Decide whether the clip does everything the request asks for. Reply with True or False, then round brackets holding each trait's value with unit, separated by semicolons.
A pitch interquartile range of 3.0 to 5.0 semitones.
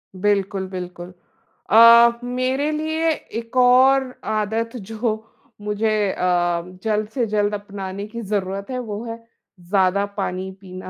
True (3.5 semitones)